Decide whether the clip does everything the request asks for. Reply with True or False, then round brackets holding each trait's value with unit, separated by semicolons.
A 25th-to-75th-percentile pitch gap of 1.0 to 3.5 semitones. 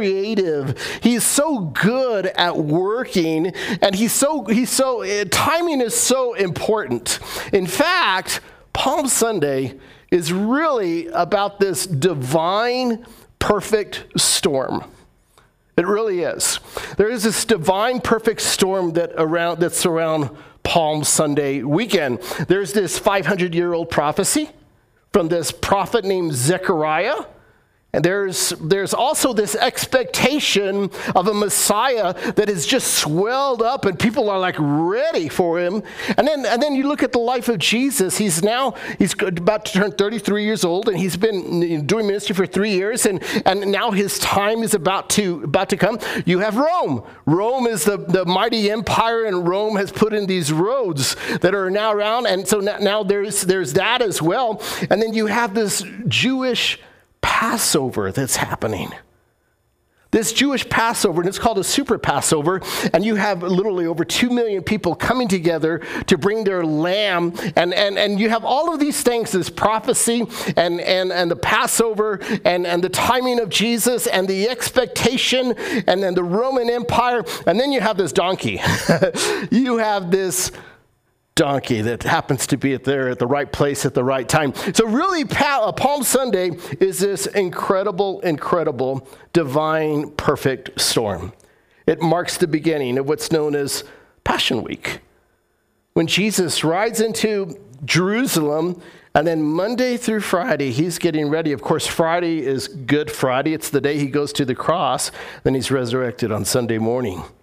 False (5.1 semitones)